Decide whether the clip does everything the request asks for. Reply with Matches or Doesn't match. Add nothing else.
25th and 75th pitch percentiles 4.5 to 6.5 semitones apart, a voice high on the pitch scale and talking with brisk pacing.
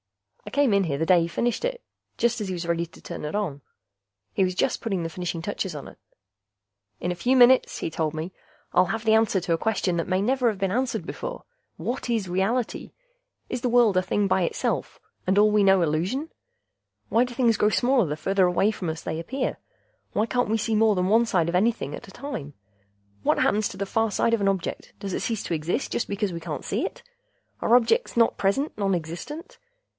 Matches